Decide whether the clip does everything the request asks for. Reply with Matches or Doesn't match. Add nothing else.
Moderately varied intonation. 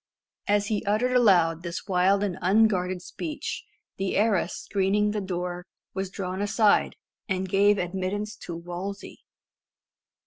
Doesn't match